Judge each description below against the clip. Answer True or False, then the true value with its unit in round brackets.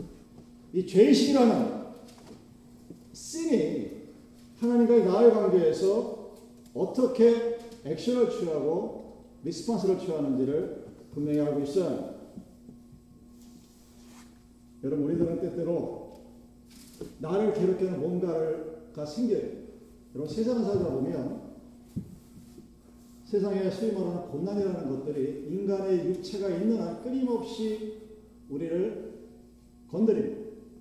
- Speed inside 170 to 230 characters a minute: True (220 characters per minute)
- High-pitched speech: True (195 Hz)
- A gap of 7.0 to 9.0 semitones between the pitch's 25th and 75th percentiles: True (7.4 semitones)